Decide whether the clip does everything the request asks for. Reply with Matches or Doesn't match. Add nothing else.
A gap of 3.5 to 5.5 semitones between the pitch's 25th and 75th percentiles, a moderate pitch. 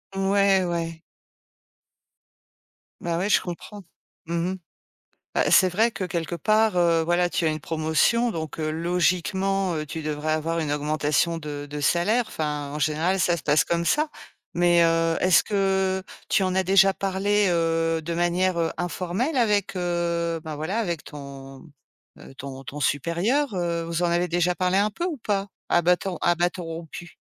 Doesn't match